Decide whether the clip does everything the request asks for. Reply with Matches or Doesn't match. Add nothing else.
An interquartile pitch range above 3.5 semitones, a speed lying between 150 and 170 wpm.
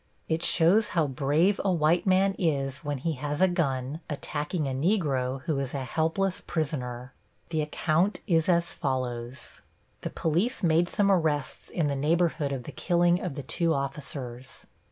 Matches